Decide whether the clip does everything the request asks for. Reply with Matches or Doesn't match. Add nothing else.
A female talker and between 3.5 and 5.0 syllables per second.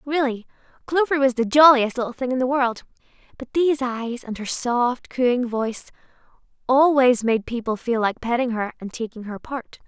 Matches